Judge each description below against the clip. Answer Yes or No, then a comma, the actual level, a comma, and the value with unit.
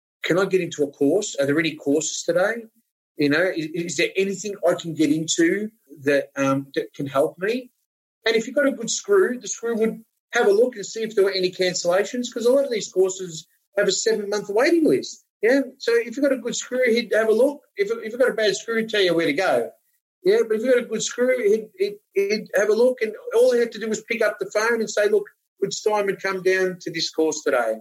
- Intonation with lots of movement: Yes, wide, 6.4 semitones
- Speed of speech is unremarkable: No, fast, 255 wpm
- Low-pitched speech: No, high, 215 Hz